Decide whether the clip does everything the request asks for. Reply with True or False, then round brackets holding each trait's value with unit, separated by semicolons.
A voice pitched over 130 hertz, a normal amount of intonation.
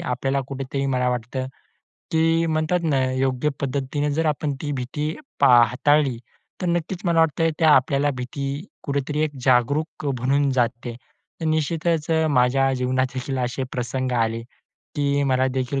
True (140 Hz; 3.0 semitones)